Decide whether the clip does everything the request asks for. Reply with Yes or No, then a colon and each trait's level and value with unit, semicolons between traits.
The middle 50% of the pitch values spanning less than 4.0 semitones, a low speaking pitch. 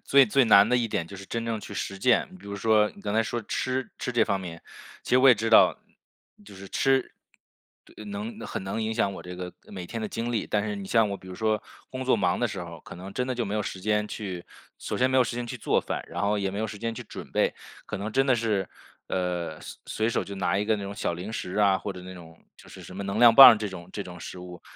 Yes: average, 3.4 semitones; low, 105 Hz